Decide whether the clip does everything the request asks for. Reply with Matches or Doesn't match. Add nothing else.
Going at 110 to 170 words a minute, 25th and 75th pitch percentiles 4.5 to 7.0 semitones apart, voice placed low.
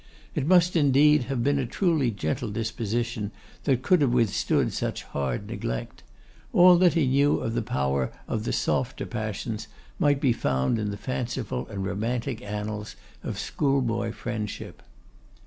Matches